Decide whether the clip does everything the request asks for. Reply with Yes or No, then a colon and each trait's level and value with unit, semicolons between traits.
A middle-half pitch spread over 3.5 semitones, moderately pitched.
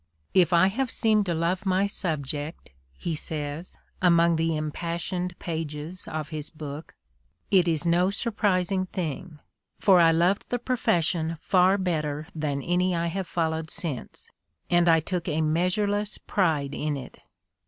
No: average, 2.9 semitones; medium, 170 Hz